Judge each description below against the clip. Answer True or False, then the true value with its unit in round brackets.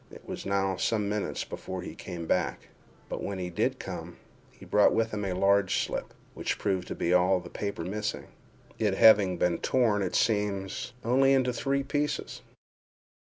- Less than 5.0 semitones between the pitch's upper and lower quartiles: True (3.2 semitones)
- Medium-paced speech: True (165 wpm)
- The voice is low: True (100 Hz)